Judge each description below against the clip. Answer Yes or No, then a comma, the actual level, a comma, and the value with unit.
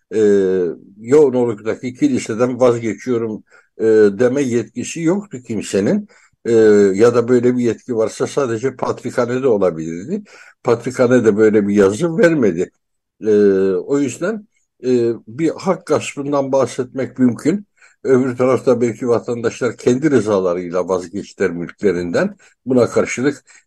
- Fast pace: No, average, 100 wpm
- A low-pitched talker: Yes, low, 120 Hz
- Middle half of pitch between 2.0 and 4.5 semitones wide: Yes, average, 3.6 semitones